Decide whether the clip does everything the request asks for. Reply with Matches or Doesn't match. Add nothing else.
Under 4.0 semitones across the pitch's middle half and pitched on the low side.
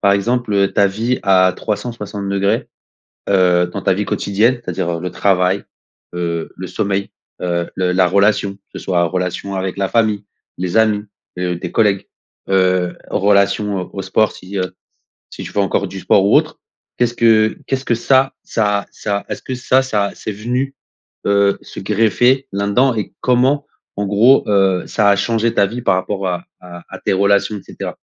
Matches